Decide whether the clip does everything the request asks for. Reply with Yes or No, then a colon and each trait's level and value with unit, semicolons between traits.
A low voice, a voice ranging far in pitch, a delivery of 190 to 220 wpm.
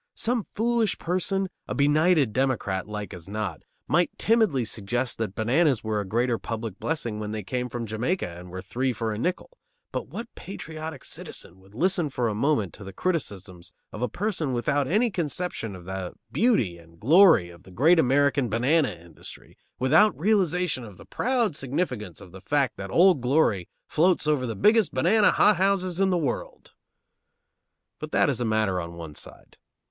No: low, 130 Hz; wide, 9.0 semitones; average, 175 wpm